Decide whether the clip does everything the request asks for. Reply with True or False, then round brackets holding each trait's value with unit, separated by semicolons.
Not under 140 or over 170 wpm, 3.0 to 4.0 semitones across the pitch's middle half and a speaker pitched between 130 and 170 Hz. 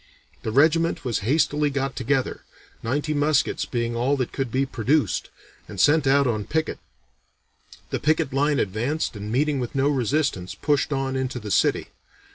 True (160 wpm; 3.7 semitones; 135 Hz)